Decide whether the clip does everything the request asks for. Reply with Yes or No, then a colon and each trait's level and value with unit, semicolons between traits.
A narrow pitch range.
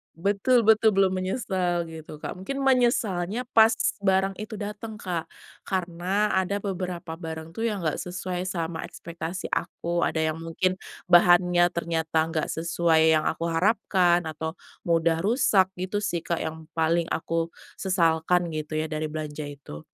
No: average, 3.0 semitones